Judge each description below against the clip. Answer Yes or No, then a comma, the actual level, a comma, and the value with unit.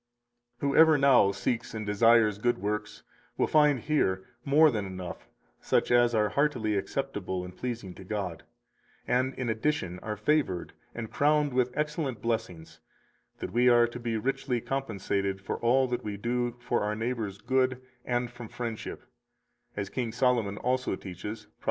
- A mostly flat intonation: No, average, 3.7 semitones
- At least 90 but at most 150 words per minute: No, average, 160 wpm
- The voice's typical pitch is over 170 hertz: No, low, 115 Hz